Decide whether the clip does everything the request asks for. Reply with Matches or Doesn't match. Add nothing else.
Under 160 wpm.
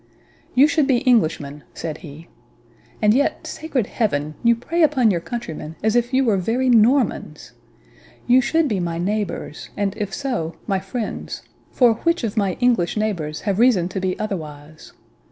Doesn't match